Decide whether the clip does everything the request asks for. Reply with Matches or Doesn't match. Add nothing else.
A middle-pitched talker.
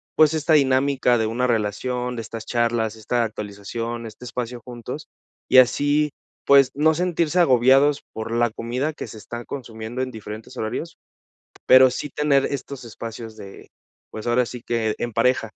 Doesn't match